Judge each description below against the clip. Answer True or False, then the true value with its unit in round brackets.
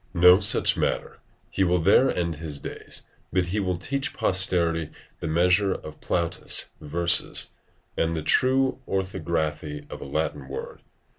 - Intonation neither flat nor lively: True (3.2 semitones)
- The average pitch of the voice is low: True (85 Hz)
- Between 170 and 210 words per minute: False (145 wpm)